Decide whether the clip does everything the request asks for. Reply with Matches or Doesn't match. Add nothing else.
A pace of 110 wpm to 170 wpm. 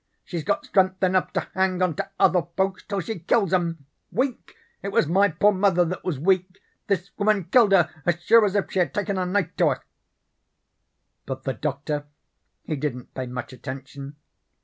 Doesn't match